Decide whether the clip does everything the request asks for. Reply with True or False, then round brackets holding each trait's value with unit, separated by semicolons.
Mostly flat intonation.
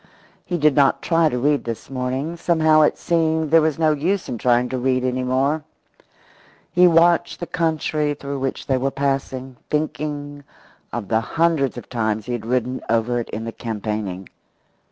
False (4.2 semitones)